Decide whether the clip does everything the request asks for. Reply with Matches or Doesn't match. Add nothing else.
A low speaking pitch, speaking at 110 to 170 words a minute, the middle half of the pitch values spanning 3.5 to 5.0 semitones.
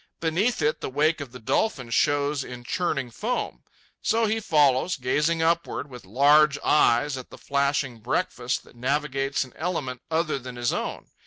Doesn't match